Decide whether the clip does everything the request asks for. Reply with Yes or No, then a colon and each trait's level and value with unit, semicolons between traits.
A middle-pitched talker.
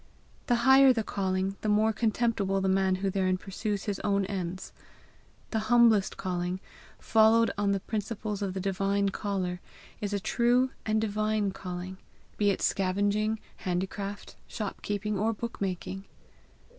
No: high, 200 Hz